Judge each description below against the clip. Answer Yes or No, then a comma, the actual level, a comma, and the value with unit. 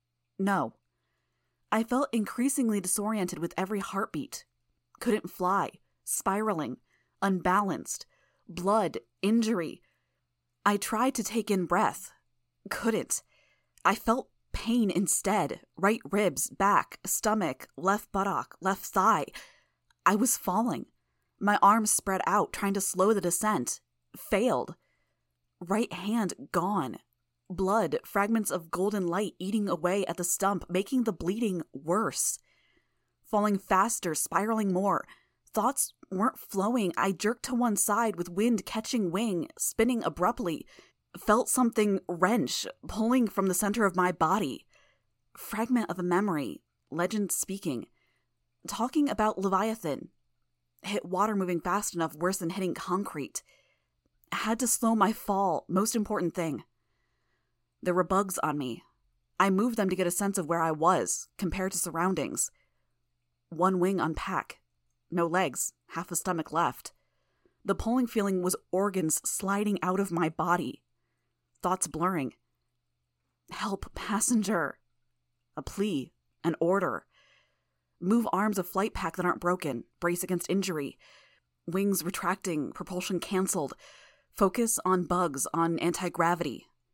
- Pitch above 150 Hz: Yes, high, 190 Hz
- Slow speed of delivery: Yes, slow, 125 wpm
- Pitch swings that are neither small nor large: Yes, average, 3.8 semitones